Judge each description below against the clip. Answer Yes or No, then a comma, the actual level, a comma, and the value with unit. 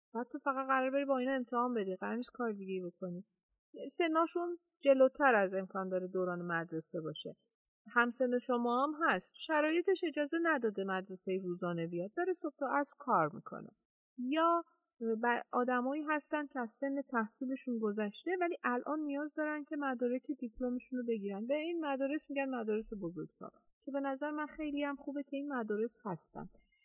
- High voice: Yes, very high, 260 Hz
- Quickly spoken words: Yes, fast, 160 wpm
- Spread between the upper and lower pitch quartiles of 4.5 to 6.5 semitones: Yes, average, 5.2 semitones